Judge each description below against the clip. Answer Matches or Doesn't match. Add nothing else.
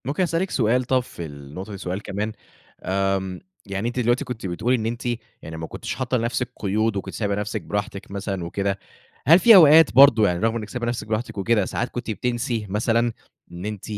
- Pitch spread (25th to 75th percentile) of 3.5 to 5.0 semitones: Matches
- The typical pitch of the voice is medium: Doesn't match